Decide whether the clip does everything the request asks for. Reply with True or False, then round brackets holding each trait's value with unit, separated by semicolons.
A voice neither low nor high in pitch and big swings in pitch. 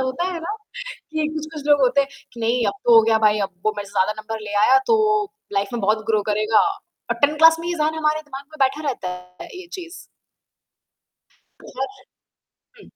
False (265 Hz; 6.4 semitones)